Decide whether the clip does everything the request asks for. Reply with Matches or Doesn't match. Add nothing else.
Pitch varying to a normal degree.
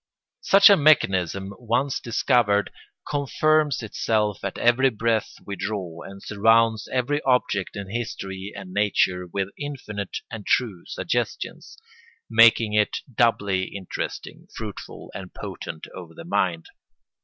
Matches